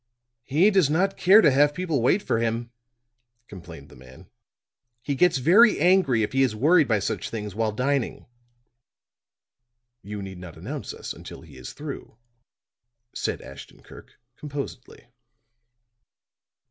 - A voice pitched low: Yes, low, 130 Hz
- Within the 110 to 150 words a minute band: Yes, average, 140 wpm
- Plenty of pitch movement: Yes, wide, 7.2 semitones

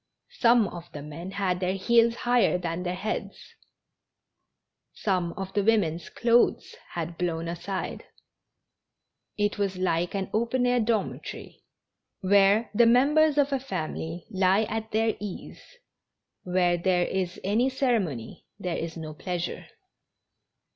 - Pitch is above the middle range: Yes, high, 195 Hz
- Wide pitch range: No, average, 4.6 semitones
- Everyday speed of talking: No, slow, 130 wpm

